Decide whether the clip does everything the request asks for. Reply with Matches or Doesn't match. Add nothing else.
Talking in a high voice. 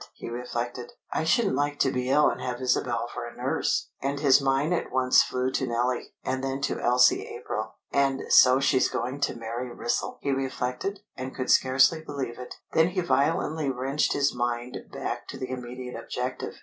Doesn't match